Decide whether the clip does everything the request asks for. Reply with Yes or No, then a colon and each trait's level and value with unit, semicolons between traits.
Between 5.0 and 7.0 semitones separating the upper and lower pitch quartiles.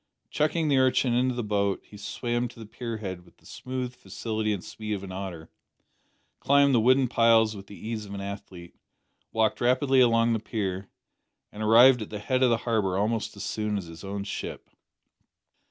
No: average, 3.6 semitones